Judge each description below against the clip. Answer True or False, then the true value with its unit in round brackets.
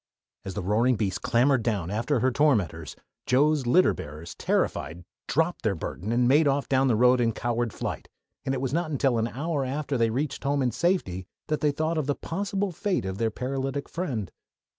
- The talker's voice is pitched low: True (130 Hz)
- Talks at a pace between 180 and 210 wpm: True (205 wpm)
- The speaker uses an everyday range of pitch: True (4.7 semitones)